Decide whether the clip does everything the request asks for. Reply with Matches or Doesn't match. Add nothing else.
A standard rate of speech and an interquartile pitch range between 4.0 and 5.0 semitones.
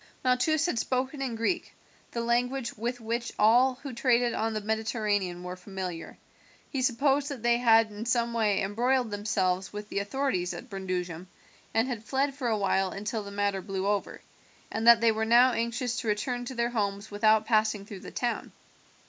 Doesn't match